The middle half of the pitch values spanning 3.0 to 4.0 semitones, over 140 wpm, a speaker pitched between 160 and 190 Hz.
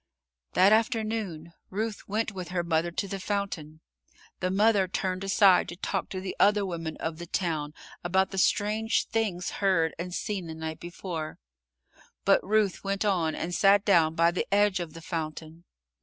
Yes: average, 3.3 semitones; average, 170 wpm; medium, 185 Hz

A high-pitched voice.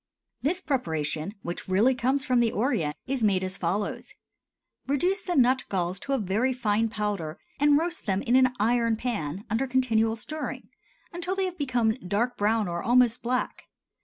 Yes: high, 235 Hz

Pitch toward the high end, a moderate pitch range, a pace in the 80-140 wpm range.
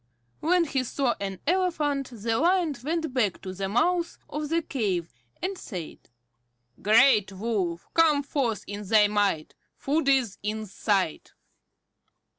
No: high, 240 Hz; wide, 7.0 semitones; slow, 135 wpm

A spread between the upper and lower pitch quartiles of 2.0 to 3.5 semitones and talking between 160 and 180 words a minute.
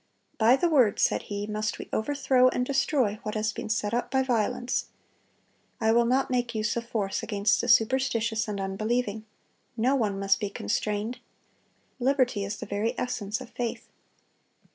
Yes: average, 3.0 semitones; average, 165 wpm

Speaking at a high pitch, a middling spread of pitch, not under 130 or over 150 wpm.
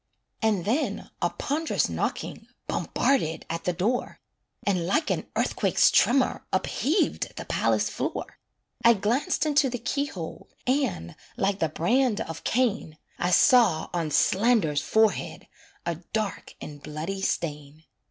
No: high, 205 Hz; wide, 7.2 semitones; slow, 135 wpm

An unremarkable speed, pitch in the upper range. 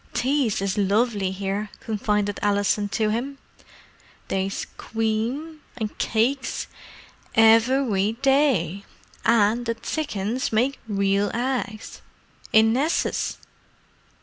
No: slow, 90 wpm; high, 220 Hz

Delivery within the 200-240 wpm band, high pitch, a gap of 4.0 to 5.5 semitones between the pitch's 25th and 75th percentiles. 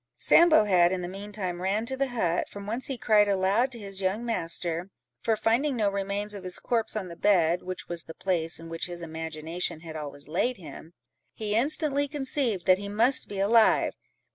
Yes: fast, 205 wpm; high, 200 Hz; average, 4.7 semitones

